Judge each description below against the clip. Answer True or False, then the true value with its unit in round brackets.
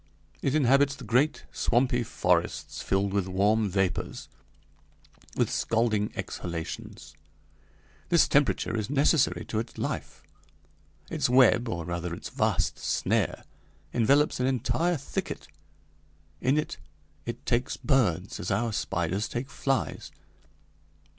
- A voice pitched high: False (115 Hz)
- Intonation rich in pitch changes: True (5.7 semitones)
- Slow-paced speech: True (115 wpm)